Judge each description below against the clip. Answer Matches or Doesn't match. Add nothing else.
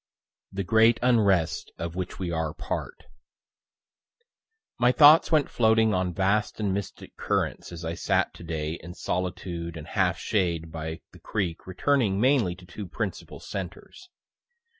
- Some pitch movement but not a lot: Matches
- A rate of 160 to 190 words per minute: Doesn't match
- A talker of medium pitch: Doesn't match